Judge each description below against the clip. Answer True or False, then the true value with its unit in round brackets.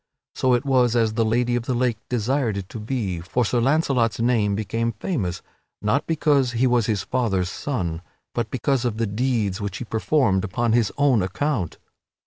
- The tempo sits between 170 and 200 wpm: True (185 wpm)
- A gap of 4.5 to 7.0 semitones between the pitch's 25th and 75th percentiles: False (3.5 semitones)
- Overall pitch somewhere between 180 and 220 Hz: False (115 Hz)